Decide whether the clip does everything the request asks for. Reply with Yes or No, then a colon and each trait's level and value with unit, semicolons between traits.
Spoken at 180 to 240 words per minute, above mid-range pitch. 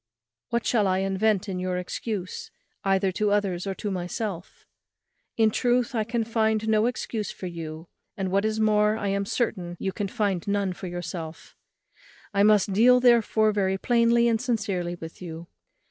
No: average, 170 wpm; high, 200 Hz